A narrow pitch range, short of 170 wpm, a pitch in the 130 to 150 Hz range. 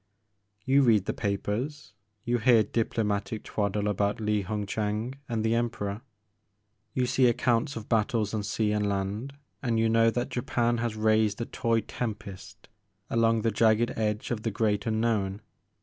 No: narrow, 2.1 semitones; average, 160 wpm; low, 110 Hz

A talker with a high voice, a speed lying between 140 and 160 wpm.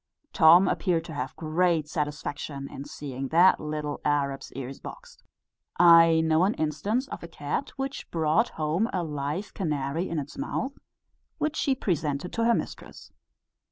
No: medium, 160 Hz; average, 155 wpm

